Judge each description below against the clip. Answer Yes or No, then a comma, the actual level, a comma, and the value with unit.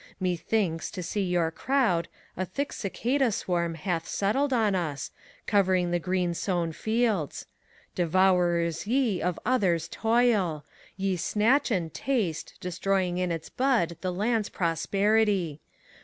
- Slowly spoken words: Yes, slow, 125 wpm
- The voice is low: No, medium, 185 Hz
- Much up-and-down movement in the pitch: No, average, 4.3 semitones